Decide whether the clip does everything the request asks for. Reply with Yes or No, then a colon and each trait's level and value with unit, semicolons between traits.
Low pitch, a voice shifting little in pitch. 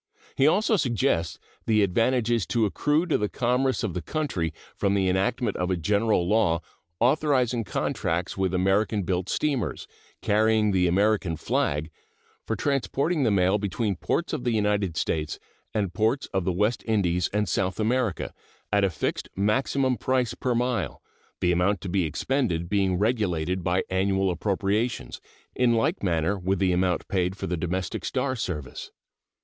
No: low, 100 Hz; average, 4.7 semitones